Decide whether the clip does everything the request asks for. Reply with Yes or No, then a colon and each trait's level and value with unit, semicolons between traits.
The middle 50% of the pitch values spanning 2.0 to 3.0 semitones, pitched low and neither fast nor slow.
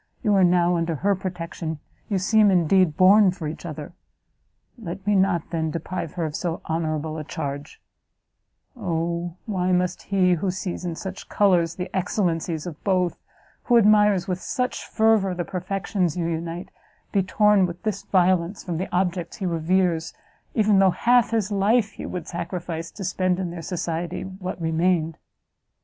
No: average, 2.7 semitones; medium, 180 Hz; average, 165 wpm